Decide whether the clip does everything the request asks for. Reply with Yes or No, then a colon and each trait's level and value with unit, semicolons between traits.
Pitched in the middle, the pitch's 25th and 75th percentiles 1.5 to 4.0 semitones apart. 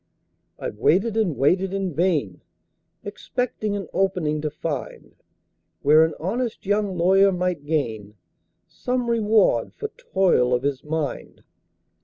No: medium, 180 Hz; wide, 5.5 semitones